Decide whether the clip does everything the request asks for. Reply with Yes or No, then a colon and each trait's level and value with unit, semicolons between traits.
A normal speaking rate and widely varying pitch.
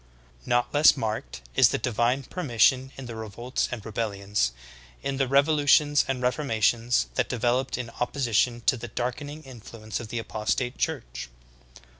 No: average, 155 wpm; average, 3.2 semitones